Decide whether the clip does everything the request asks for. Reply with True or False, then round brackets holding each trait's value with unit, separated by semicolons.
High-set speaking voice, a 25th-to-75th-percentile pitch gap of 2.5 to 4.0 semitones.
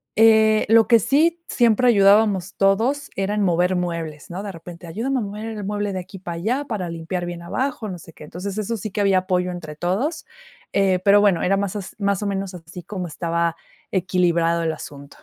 True (195 Hz; 3.5 semitones)